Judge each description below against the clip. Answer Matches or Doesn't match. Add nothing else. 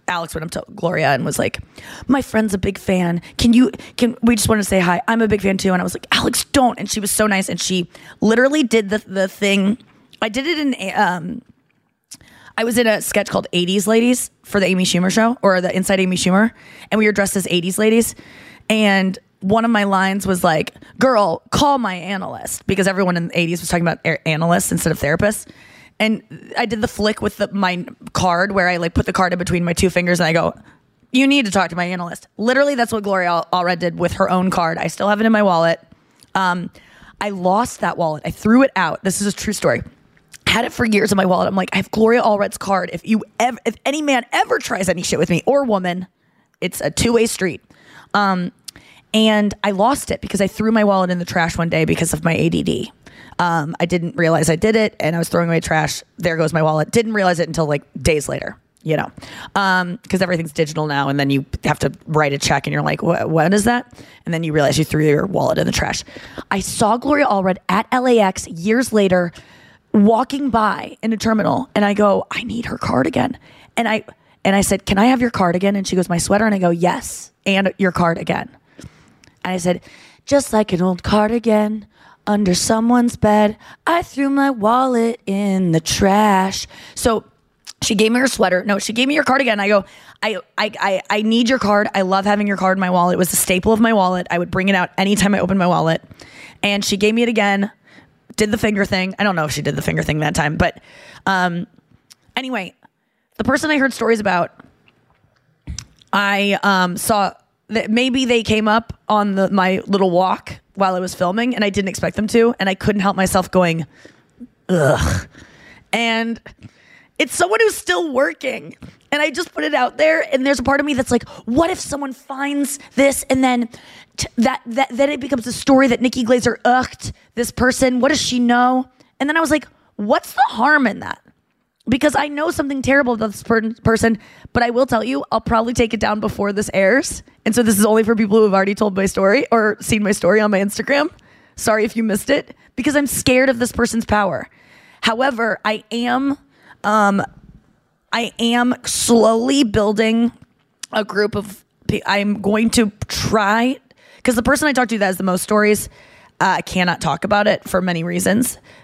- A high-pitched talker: Matches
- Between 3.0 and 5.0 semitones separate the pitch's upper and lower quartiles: Matches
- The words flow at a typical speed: Doesn't match